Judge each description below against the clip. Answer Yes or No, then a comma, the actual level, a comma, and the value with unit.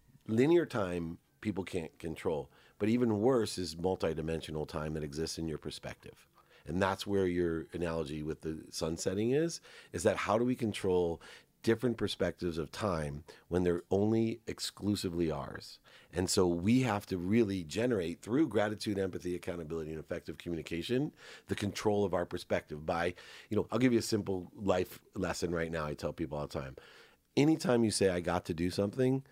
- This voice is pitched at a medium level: No, very low, 90 Hz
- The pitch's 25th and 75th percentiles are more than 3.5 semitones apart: Yes, average, 4.5 semitones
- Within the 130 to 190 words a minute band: Yes, average, 175 wpm